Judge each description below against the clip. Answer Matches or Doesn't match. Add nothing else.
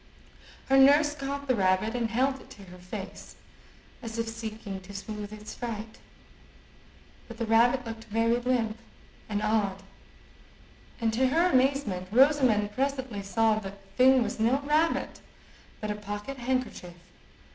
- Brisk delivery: Doesn't match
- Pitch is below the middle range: Doesn't match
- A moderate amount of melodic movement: Matches